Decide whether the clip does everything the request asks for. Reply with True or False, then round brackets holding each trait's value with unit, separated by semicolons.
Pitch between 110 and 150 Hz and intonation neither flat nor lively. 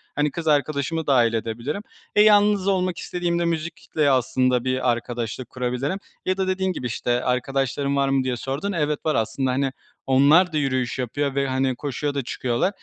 True (140 Hz; 4.4 semitones)